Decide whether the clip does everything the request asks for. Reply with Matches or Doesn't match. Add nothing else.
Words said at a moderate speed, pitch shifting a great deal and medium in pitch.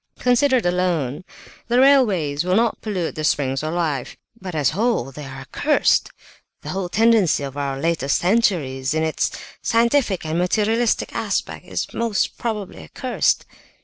Matches